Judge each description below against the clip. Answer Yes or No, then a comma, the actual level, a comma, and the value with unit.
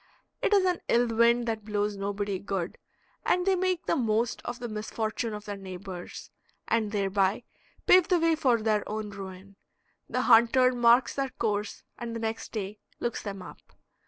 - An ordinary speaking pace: Yes, average, 175 wpm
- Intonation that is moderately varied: Yes, average, 3.1 semitones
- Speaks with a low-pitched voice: No, high, 220 Hz